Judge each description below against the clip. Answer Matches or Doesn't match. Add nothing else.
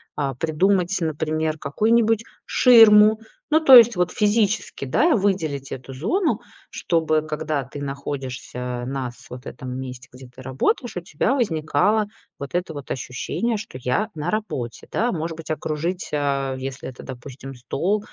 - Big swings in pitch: Matches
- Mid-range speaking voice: Matches